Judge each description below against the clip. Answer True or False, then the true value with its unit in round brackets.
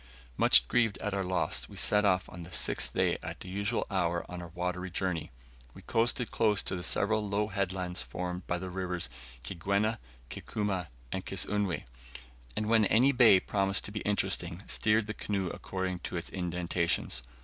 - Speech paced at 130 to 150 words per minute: False (175 wpm)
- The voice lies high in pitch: False (95 Hz)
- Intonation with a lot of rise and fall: False (2.7 semitones)